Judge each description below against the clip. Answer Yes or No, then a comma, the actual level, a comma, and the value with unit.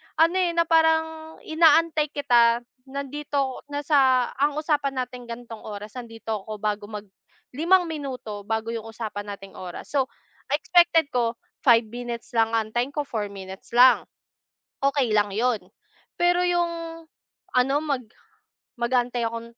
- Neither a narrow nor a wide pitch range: Yes, average, 4.9 semitones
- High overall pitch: Yes, very high, 250 Hz